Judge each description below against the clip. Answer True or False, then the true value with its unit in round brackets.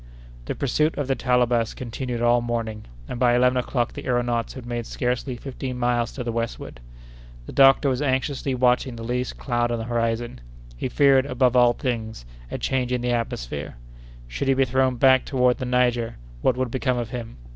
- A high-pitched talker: False (125 Hz)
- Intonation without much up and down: True (1.6 semitones)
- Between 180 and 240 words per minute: True (195 wpm)